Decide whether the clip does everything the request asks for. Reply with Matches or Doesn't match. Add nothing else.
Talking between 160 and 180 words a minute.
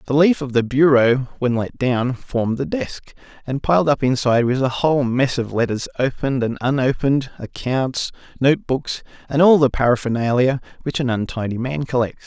Matches